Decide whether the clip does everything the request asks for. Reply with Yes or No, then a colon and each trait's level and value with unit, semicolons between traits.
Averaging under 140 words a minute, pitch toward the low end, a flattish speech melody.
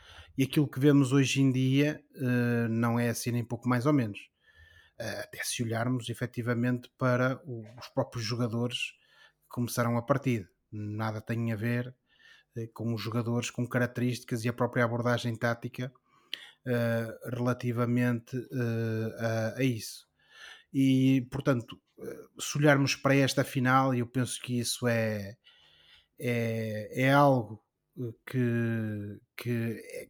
Yes: average, 125 wpm; low, 120 Hz; narrow, 1.9 semitones